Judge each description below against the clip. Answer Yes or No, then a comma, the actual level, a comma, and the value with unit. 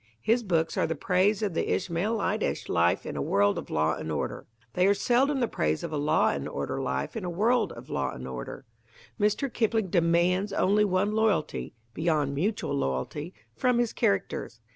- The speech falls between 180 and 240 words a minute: Yes, average, 185 wpm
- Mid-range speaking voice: Yes, medium, 180 Hz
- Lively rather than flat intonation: Yes, wide, 7.1 semitones